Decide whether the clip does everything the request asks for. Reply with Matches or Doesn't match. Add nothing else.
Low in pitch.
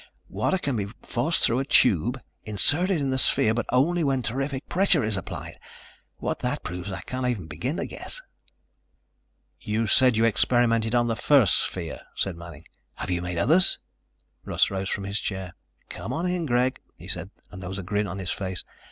Matches